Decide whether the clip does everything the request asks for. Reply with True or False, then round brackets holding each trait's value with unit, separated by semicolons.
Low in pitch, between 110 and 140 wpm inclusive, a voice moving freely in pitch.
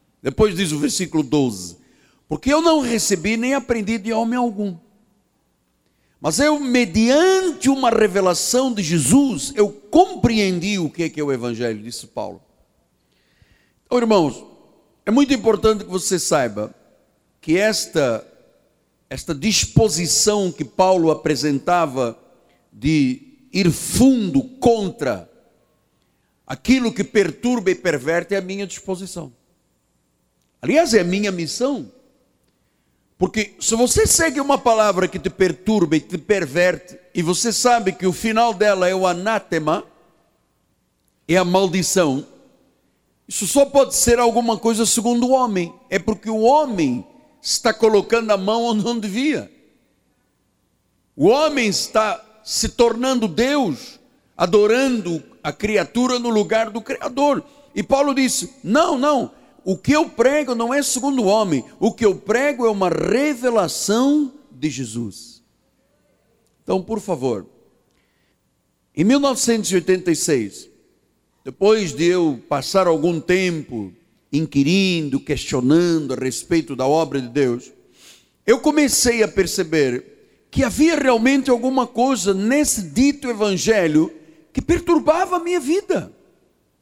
False (215 Hz; 125 wpm; 6.6 semitones)